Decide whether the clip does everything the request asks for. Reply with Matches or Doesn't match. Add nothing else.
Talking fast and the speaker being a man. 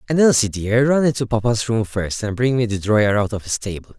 Matches